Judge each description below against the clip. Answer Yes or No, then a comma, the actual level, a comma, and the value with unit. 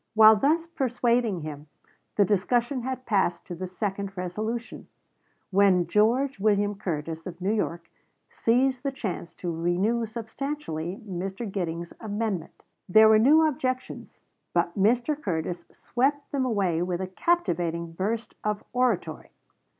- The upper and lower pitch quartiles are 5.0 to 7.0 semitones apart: Yes, wide, 5.5 semitones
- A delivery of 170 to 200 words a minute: No, slow, 135 wpm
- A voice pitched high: Yes, high, 205 Hz